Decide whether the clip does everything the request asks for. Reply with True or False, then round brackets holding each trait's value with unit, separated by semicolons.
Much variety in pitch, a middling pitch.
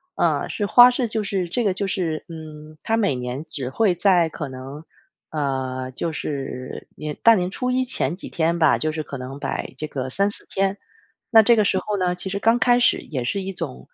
True (6.3 semitones; 170 Hz)